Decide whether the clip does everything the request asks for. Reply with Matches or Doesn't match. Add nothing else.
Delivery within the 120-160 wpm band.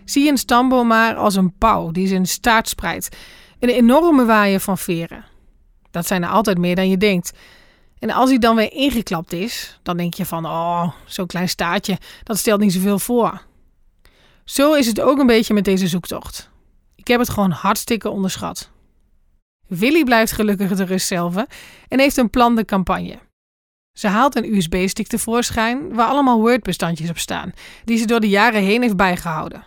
Doesn't match